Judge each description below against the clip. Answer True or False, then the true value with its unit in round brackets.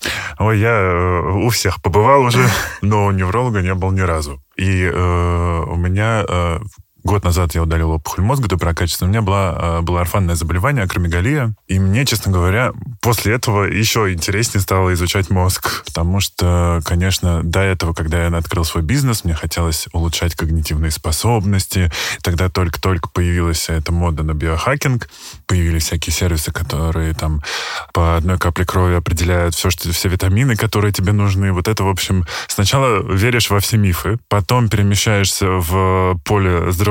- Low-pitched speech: True (95 Hz)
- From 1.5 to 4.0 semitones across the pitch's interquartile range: True (3.1 semitones)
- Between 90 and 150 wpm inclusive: False (160 wpm)